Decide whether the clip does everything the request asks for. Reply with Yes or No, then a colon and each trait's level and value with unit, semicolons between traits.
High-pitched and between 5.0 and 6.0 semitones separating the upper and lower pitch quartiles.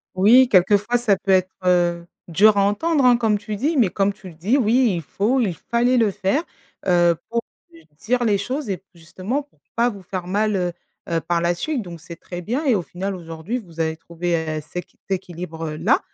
Yes: high, 195 Hz; average, 5.3 semitones